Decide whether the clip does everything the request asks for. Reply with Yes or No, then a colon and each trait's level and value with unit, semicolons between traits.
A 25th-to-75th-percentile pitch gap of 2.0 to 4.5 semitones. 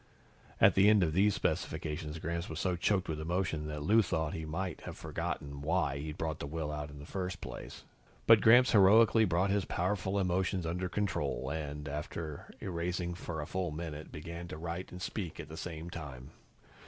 Yes: average, 3.5 semitones